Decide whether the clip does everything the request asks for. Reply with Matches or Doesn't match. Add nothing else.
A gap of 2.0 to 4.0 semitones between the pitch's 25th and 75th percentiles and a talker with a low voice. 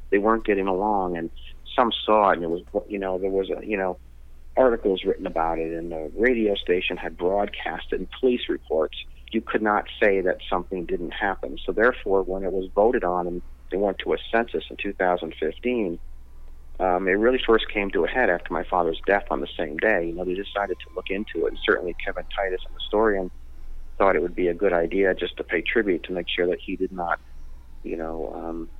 Doesn't match